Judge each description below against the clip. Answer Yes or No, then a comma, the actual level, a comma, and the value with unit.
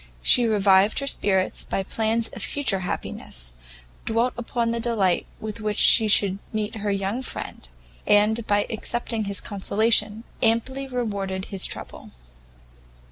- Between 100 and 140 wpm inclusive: Yes, slow, 135 wpm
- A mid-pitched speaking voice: No, high, 215 Hz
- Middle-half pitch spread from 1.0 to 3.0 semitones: Yes, average, 2.7 semitones